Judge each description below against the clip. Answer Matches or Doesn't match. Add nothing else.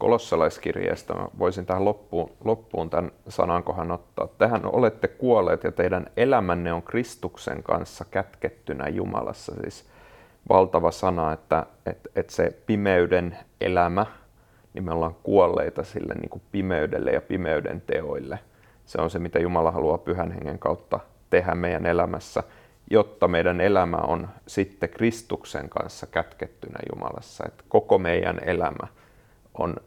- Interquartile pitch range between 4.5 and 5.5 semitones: Matches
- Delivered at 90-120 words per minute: Doesn't match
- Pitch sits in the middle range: Doesn't match